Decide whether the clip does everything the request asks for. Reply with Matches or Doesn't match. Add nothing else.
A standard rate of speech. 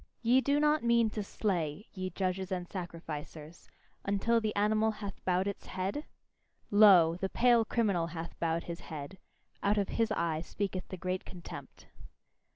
Matches